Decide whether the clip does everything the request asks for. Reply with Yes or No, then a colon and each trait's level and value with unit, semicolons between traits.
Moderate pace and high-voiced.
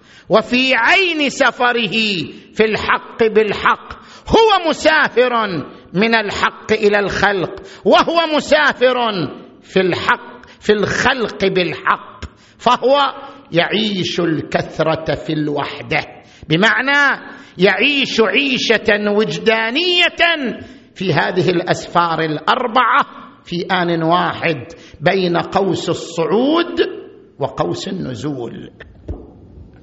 Yes: average, 80 wpm; high, 210 Hz